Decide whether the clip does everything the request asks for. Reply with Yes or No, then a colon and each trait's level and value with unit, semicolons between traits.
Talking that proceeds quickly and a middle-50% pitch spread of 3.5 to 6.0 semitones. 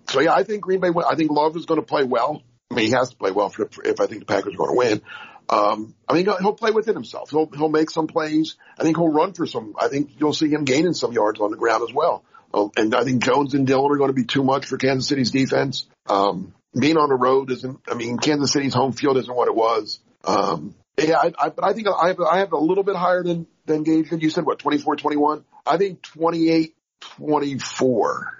Yes: fast, 255 wpm; average, 3.9 semitones